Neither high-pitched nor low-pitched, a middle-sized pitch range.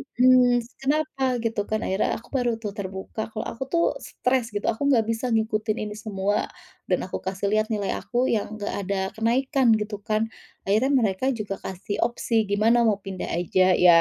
No: high, 215 Hz; average, 3.2 semitones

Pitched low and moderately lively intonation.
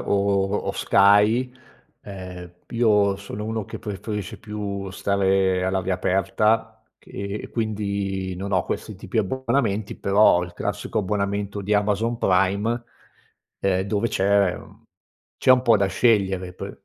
No: low, 100 Hz; narrow, 1.7 semitones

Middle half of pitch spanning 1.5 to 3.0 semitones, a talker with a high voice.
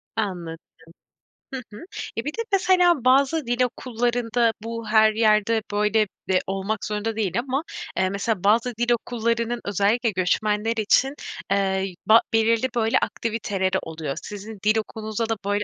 Yes: narrow, 2.6 semitones; high, 220 Hz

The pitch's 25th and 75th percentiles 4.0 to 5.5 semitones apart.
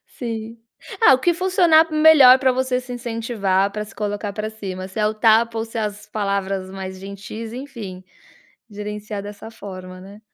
No: average, 3.6 semitones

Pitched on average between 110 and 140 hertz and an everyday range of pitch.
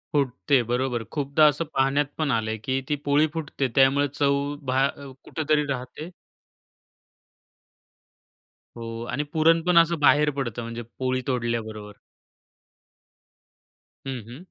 Yes: low, 135 Hz; average, 3.4 semitones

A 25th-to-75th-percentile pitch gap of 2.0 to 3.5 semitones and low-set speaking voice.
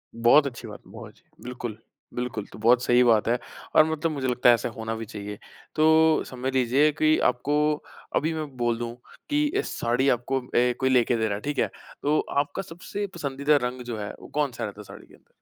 No: average, 4.0 semitones; low, 125 Hz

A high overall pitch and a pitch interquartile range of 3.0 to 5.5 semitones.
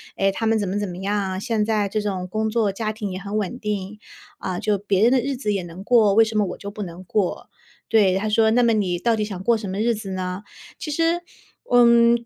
No: high, 210 Hz; narrow, 2.6 semitones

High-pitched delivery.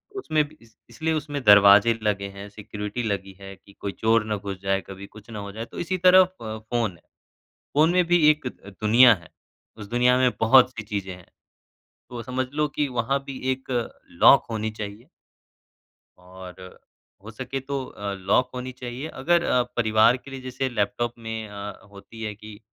No: low, 115 Hz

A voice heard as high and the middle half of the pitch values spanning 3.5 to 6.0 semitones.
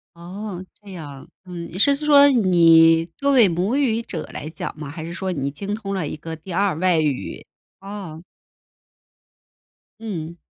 No: medium, 180 Hz; average, 4.1 semitones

